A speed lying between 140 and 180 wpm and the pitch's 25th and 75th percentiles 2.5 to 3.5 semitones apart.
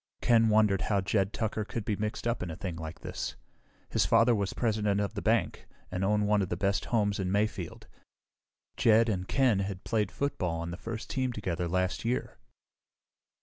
No: average, 190 wpm; average, 3.0 semitones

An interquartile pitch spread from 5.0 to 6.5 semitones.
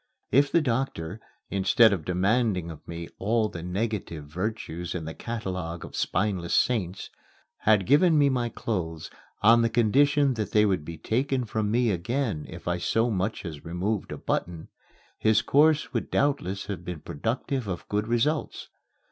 Yes: average, 5.3 semitones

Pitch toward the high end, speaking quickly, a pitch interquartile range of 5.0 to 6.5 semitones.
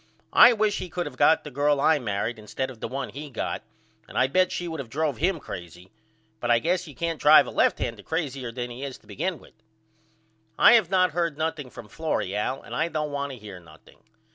No: medium, 145 Hz; fast, 235 wpm; average, 5.3 semitones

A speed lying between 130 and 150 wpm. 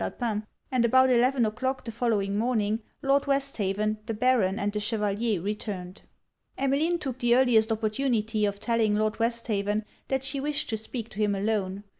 No: average, 165 wpm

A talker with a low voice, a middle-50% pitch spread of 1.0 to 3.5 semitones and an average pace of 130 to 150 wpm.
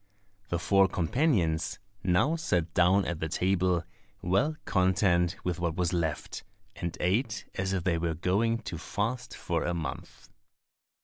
Yes: very low, 90 Hz; average, 2.7 semitones; average, 145 wpm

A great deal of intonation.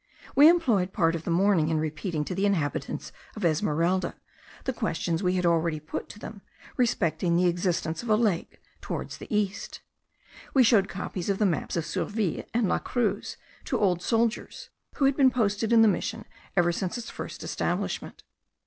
No: average, 4.8 semitones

